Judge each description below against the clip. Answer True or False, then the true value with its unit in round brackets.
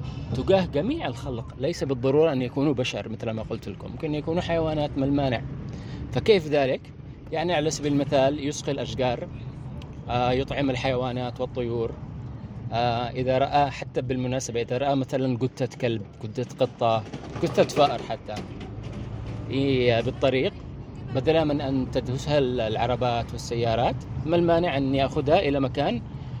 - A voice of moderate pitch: False (130 Hz)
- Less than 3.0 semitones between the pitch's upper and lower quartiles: True (2.6 semitones)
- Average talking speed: False (130 wpm)